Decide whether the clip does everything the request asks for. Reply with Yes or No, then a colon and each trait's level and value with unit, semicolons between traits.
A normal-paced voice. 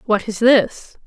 Yes: average, 170 wpm